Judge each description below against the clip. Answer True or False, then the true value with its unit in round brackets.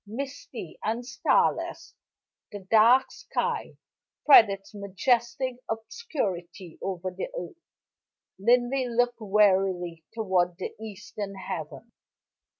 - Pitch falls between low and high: False (215 Hz)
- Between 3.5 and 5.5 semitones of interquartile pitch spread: True (4.3 semitones)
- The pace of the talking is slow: True (95 wpm)